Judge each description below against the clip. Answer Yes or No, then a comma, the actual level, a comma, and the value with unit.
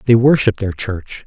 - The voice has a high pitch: No, low, 110 Hz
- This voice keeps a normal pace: Yes, average, 190 wpm